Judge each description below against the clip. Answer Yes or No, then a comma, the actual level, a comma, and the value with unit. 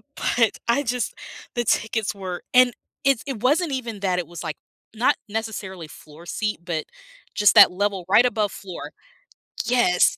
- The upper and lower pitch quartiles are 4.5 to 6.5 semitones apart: Yes, average, 4.8 semitones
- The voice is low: No, high, 210 Hz